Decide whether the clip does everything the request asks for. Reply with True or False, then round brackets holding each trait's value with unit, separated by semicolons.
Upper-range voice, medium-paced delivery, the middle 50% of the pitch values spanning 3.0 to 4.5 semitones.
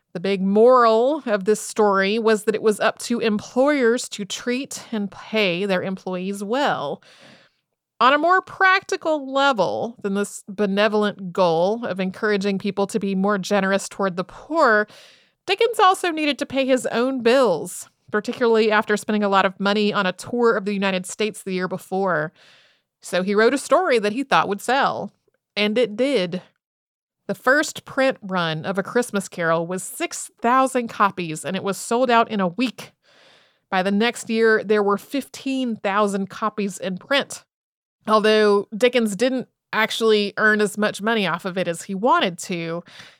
True (210 Hz; 170 wpm; 3.8 semitones)